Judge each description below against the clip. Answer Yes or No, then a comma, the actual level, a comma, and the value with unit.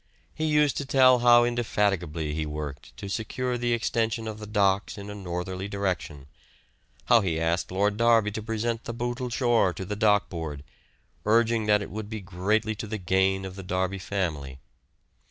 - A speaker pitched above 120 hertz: No, low, 105 Hz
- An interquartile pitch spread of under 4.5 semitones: Yes, average, 3.8 semitones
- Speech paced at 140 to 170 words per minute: No, average, 180 wpm